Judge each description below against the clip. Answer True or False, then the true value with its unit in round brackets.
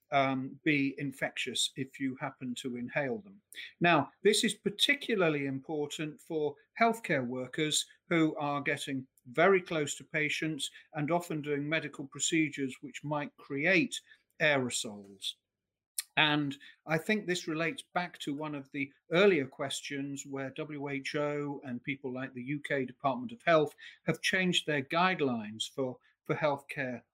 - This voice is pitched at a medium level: True (145 Hz)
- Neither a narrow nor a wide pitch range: True (3.2 semitones)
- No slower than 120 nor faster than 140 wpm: True (135 wpm)